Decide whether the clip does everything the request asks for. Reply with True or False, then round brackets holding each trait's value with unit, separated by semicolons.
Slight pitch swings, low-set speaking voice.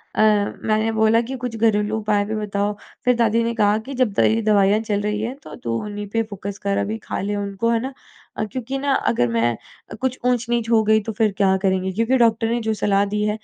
False (2.1 semitones; 215 Hz)